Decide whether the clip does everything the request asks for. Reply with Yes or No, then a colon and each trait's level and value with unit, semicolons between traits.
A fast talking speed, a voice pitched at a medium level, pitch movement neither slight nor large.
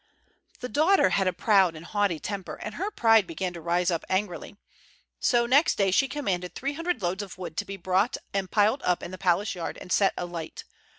No: fast, 215 wpm; high, 195 Hz; average, 3.9 semitones